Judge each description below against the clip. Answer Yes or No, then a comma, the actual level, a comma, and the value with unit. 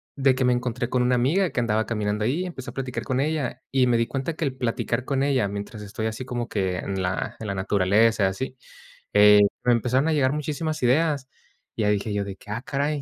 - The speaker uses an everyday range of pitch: Yes, average, 4.1 semitones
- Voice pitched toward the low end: Yes, low, 125 Hz